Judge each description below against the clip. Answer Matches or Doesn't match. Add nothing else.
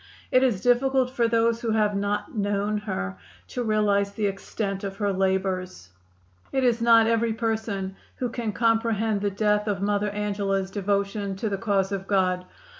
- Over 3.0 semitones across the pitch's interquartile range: Doesn't match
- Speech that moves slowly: Doesn't match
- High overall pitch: Matches